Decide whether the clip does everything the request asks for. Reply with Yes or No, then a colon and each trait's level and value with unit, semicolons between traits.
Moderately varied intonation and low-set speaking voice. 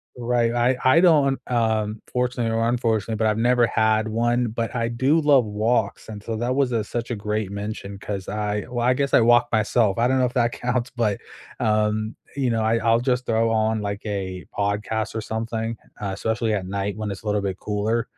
No: narrow, 2.3 semitones; low, 115 Hz